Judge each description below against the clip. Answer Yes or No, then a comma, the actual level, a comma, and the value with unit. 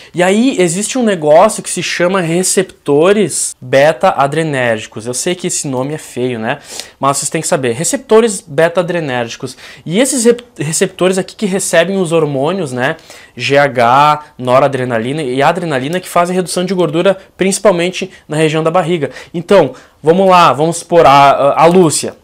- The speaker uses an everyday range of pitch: Yes, average, 4.9 semitones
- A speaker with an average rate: Yes, average, 155 wpm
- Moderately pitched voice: Yes, medium, 170 Hz